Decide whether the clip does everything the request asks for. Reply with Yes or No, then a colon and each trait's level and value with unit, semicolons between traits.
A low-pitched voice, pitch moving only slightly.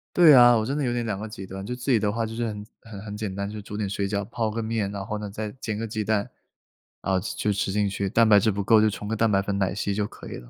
Yes: low, 105 Hz; narrow, 2.1 semitones